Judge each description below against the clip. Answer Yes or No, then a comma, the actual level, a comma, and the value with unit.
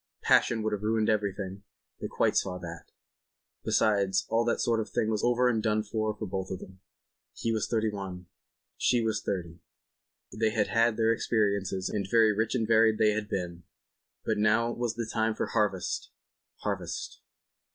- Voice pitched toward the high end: No, low, 110 Hz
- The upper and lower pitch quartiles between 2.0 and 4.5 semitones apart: Yes, narrow, 2.4 semitones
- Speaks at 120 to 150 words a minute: No, average, 165 wpm